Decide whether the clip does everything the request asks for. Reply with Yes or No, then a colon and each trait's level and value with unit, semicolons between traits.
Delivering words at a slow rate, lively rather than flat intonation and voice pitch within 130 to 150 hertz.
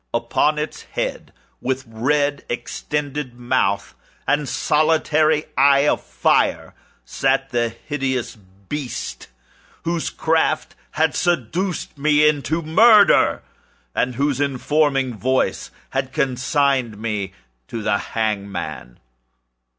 No: slow, 100 wpm; average, 4.1 semitones; low, 135 Hz